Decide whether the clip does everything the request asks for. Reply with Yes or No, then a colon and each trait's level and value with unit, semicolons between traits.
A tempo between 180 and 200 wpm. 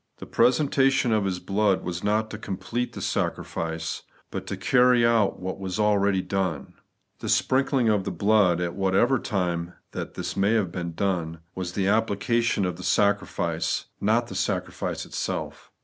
No: average, 160 wpm